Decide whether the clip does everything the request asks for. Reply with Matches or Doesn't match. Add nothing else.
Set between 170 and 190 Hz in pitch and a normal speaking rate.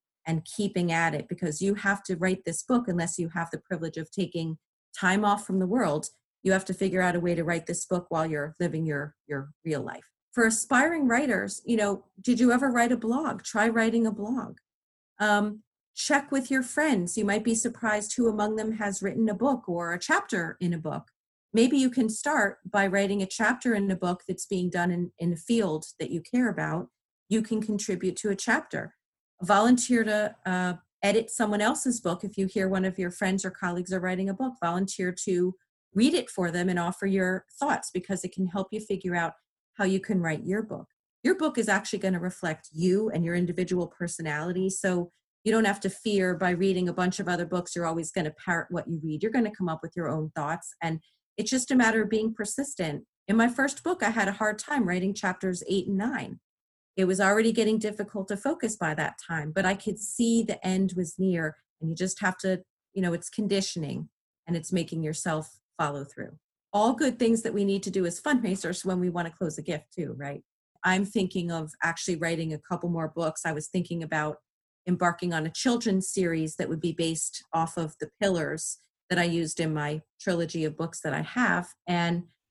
Doesn't match